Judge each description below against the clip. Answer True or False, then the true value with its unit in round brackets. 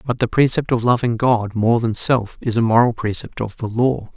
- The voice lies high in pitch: False (115 Hz)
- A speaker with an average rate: False (230 wpm)